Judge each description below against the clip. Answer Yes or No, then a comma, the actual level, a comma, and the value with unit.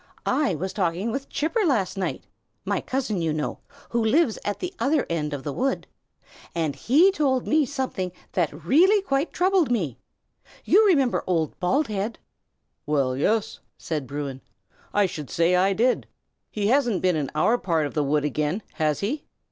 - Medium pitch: No, high, 200 Hz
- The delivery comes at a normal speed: Yes, average, 170 wpm